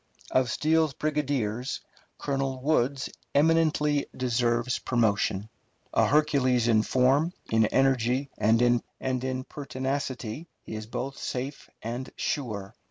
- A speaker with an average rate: No, slow, 105 wpm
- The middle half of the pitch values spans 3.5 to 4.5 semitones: No, average, 3.1 semitones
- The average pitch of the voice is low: Yes, low, 130 Hz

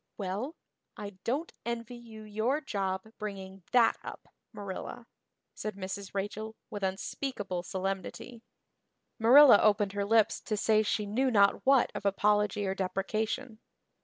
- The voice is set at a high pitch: Yes, high, 210 Hz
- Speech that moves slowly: Yes, slow, 130 wpm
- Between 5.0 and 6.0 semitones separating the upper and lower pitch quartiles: No, average, 2.8 semitones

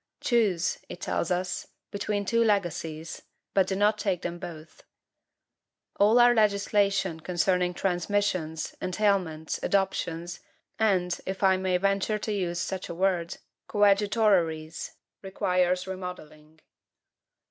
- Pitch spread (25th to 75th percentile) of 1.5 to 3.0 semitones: Yes, average, 2.7 semitones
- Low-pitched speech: No, medium, 185 Hz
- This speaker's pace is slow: Yes, slow, 115 wpm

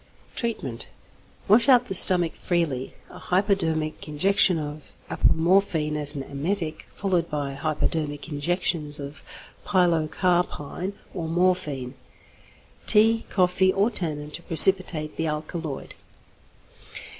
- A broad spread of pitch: No, average, 3.8 semitones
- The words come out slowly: Yes, slow, 105 wpm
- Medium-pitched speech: Yes, medium, 165 Hz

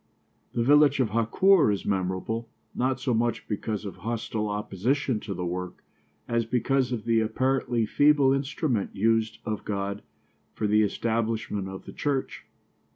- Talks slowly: No, average, 150 wpm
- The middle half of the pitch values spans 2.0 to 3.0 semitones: No, average, 3.9 semitones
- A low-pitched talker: Yes, low, 115 Hz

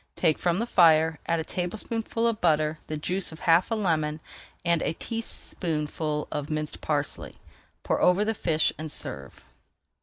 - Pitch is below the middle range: No, medium, 165 Hz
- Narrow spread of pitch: No, average, 3.2 semitones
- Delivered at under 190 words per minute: Yes, average, 160 wpm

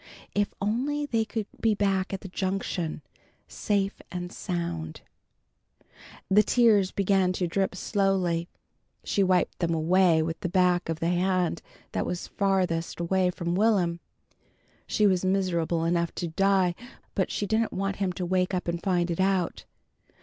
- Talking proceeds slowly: No, average, 155 wpm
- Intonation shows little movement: Yes, narrow, 2.2 semitones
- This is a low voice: No, medium, 185 Hz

